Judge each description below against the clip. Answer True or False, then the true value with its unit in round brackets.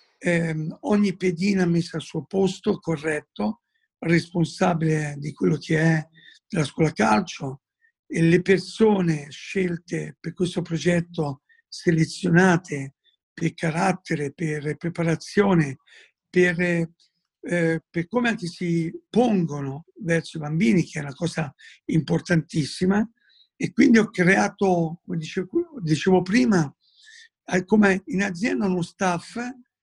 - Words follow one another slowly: True (110 wpm)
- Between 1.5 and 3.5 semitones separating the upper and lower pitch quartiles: True (3.1 semitones)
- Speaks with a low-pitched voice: False (170 Hz)